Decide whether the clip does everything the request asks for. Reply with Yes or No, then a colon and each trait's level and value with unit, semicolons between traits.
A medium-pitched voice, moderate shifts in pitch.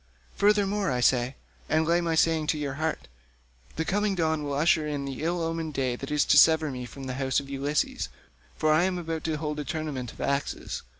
Yes: medium, 150 Hz; average, 3.4 semitones